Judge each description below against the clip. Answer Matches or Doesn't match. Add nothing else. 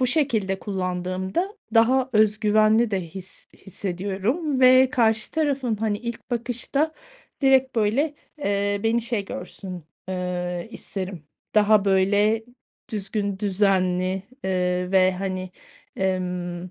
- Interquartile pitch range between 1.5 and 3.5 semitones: Doesn't match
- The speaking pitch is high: Matches